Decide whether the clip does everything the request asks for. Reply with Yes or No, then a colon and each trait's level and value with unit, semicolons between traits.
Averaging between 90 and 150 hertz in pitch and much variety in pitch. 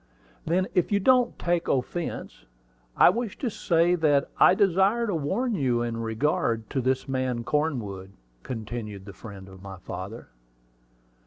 Yes: low, 135 Hz; wide, 8.0 semitones